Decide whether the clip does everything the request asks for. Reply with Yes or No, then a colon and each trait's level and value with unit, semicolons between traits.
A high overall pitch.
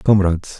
No: very low, 95 Hz